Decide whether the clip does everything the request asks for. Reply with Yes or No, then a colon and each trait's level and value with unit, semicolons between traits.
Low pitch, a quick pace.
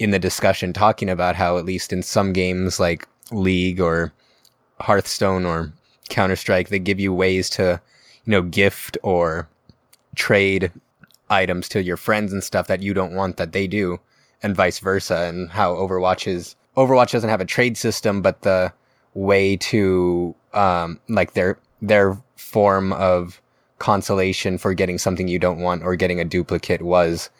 No: very low, 95 Hz; average, 165 wpm